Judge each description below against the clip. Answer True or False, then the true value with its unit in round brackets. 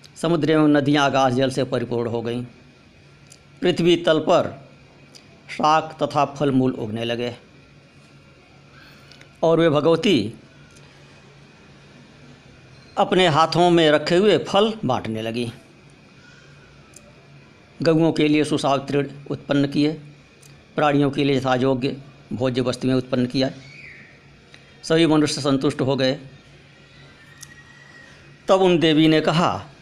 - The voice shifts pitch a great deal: False (3.3 semitones)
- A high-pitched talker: False (140 Hz)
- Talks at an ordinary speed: False (105 wpm)